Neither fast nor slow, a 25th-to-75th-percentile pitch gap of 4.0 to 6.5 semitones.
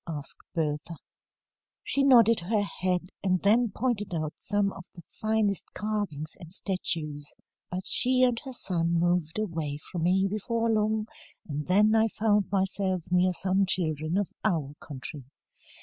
Yes: average, 150 wpm; average, 4.4 semitones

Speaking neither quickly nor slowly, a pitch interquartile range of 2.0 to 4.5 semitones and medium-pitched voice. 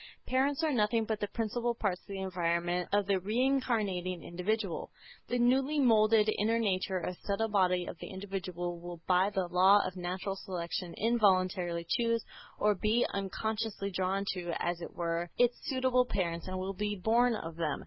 No: average, 175 wpm; average, 3.8 semitones; high, 195 Hz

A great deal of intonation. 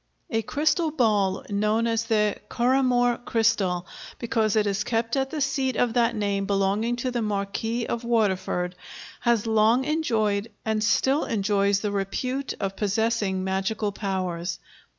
No: average, 3.2 semitones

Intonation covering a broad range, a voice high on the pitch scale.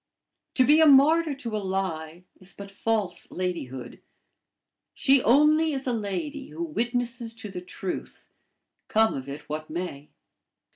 Yes: wide, 7.2 semitones; high, 220 Hz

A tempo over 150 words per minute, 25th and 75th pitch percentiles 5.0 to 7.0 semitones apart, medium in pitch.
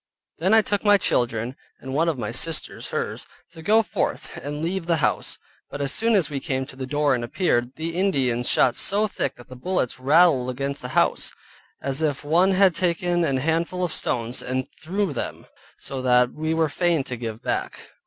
Yes: fast, 205 wpm; average, 5.3 semitones; medium, 150 Hz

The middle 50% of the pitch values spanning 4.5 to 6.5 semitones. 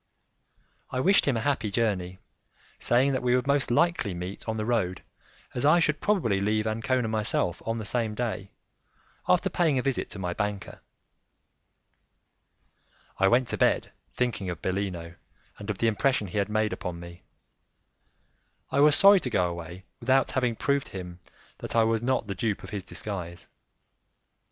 Yes: average, 4.9 semitones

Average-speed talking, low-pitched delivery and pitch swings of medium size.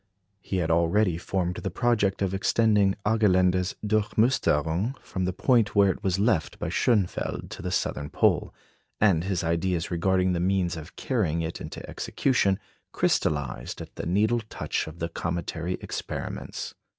Yes: average, 150 wpm; very low, 95 Hz; average, 3.4 semitones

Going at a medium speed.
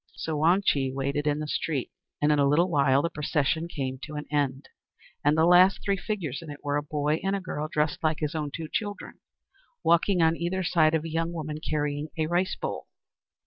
No: fast, 215 wpm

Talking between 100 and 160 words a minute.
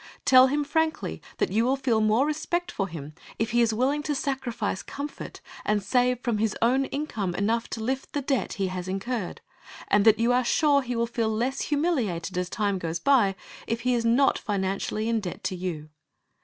No: average, 200 wpm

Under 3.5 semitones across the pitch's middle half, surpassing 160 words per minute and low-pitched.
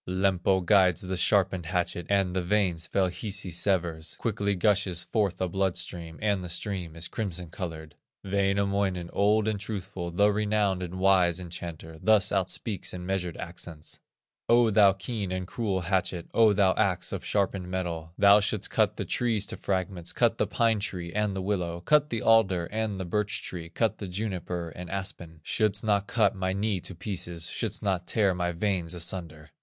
Yes: narrow, 2.6 semitones; average, 180 wpm; very low, 95 Hz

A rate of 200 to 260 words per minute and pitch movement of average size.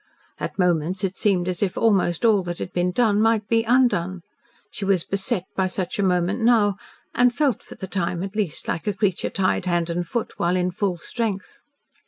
Yes: fast, 205 wpm; average, 3.2 semitones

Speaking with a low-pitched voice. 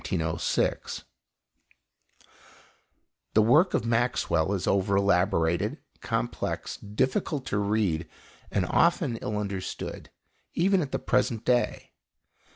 Yes: low, 105 Hz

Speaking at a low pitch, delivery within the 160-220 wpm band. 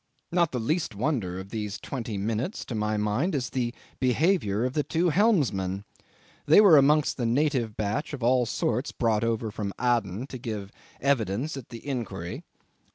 Yes: low, 120 Hz; average, 170 wpm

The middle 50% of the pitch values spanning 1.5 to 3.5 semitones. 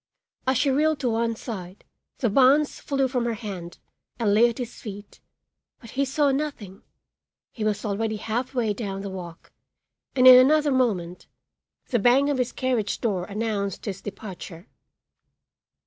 No: average, 4.4 semitones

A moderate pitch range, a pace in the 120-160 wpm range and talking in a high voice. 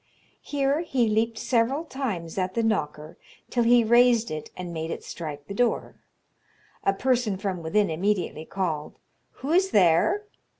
No: wide, 6.4 semitones; average, 155 wpm; high, 210 Hz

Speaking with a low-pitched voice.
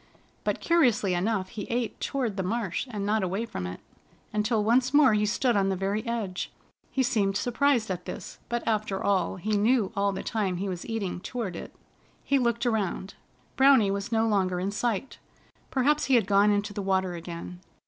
No: high, 210 Hz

